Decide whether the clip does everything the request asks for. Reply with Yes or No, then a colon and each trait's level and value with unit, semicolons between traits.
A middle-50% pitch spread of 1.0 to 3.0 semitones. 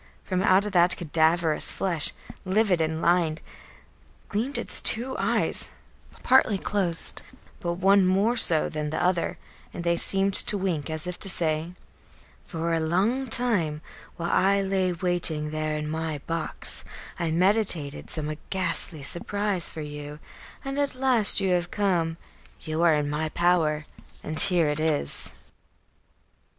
No: average, 3.7 semitones